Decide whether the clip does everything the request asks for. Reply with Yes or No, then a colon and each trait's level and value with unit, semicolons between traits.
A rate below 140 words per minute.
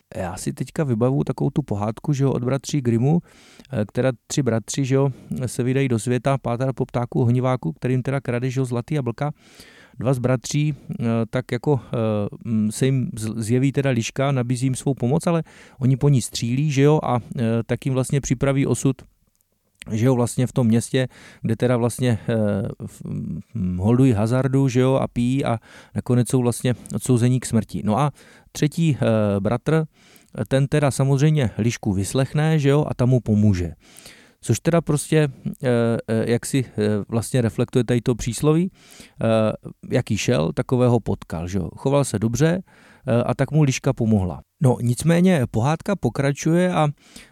No: average, 165 wpm